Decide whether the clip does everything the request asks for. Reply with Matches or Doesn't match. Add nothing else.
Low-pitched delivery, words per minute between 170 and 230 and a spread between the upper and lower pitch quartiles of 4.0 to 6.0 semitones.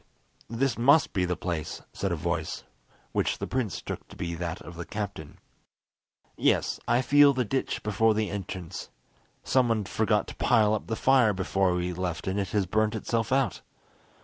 Matches